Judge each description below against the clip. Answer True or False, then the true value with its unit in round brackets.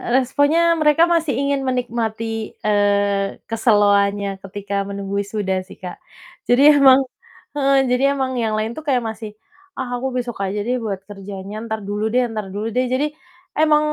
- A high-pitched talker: True (220 Hz)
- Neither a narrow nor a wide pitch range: True (4.2 semitones)